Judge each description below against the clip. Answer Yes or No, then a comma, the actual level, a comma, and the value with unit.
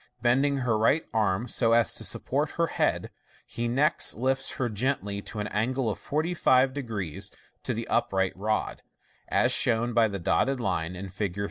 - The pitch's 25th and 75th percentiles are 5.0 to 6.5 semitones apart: No, average, 4.4 semitones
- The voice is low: Yes, low, 115 Hz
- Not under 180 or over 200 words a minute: No, average, 165 wpm